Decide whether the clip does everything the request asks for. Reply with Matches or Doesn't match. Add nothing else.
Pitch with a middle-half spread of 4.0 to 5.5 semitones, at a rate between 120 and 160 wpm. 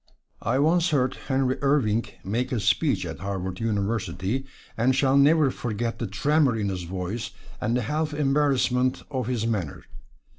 Matches